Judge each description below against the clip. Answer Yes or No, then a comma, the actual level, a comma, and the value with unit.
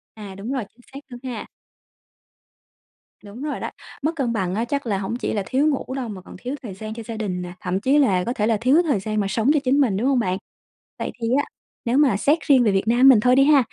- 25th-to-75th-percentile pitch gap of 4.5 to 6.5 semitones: Yes, average, 4.9 semitones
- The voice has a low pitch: No, high, 235 Hz